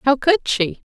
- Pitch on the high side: Yes, very high, 275 Hz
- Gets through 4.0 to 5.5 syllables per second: Yes, 4.9 syllables/s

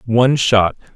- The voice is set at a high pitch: No, low, 115 Hz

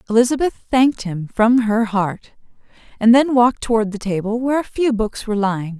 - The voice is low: No, high, 225 Hz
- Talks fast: No, average, 185 wpm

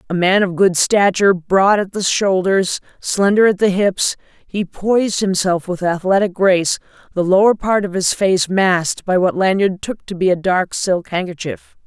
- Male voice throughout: No, female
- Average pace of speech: Yes, average, 175 wpm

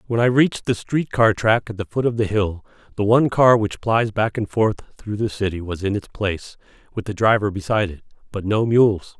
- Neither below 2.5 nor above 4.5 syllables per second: No, 5.5 syllables/s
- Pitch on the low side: Yes, low, 105 Hz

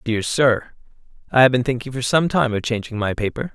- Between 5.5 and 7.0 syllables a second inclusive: Yes, 5.6 syllables/s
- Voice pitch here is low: Yes, low, 125 Hz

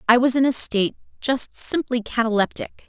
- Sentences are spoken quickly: No, average, 165 wpm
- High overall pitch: Yes, high, 240 Hz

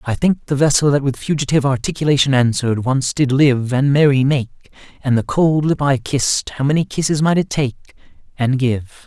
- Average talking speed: Yes, average, 185 wpm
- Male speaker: Yes, male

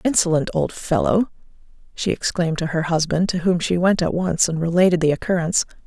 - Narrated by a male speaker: No, female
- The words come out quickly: No, average, 185 wpm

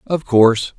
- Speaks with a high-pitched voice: No, low, 130 Hz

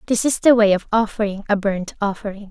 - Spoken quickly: Yes, fast, 215 wpm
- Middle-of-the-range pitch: No, high, 210 Hz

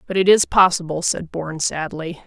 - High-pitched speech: No, medium, 170 Hz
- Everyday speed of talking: Yes, average, 185 wpm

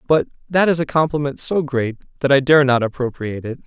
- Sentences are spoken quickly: Yes, fast, 215 wpm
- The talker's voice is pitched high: No, medium, 140 Hz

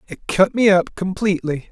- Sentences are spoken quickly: No, average, 175 wpm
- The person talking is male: Yes, male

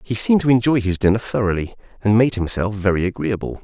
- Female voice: No, male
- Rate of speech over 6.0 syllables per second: Yes, 6.4 syllables/s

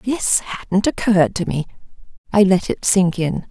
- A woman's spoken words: Yes, female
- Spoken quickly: No, average, 170 wpm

